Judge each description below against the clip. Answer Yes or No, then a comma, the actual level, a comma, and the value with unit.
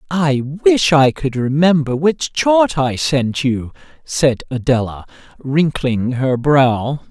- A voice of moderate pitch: Yes, medium, 145 Hz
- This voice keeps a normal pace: No, slow, 125 wpm